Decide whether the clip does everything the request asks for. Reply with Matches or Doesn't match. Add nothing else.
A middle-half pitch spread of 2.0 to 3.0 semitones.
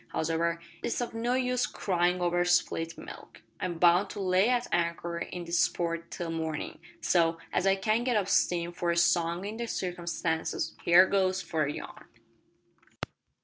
Matches